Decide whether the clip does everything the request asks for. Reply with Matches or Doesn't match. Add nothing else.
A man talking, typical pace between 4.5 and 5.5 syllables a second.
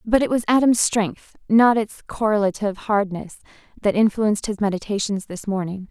Doesn't match